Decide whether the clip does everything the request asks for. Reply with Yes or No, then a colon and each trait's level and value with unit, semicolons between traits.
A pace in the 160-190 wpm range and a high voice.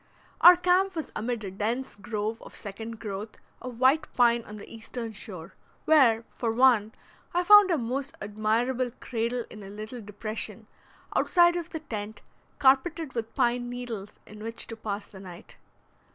Yes: average, 165 wpm; high, 230 Hz